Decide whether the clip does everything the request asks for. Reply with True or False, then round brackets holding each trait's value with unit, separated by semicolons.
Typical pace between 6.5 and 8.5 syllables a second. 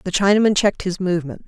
True (7.4 syllables/s)